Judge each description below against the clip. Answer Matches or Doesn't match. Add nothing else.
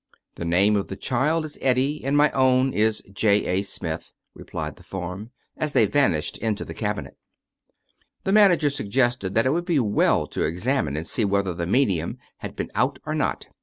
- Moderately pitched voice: Doesn't match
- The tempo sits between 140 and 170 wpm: Doesn't match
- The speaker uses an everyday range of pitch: Doesn't match